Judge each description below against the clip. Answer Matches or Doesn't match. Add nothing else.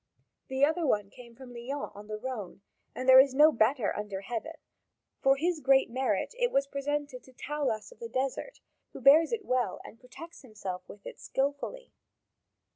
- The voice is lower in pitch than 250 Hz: Doesn't match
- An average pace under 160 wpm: Doesn't match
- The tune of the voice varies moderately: Matches